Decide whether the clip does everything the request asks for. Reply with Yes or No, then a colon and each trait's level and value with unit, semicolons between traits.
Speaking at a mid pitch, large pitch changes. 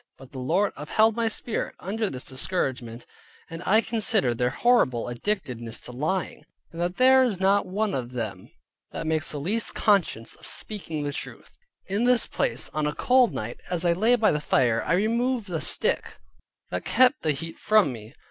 Yes: medium, 175 Hz; wide, 8.8 semitones